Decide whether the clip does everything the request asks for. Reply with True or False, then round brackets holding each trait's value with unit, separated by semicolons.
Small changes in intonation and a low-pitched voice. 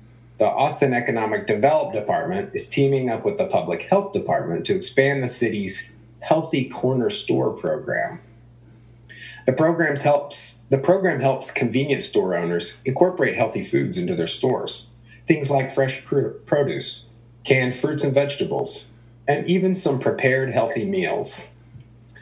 False (3.2 semitones; 130 Hz)